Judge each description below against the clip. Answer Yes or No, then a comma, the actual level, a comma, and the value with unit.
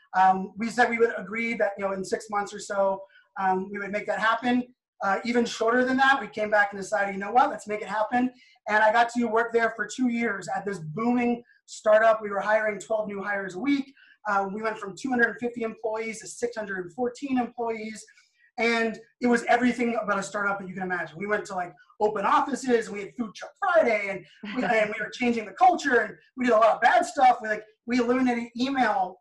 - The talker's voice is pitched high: Yes, high, 225 Hz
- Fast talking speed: Yes, fast, 240 wpm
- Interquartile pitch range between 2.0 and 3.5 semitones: Yes, average, 3.1 semitones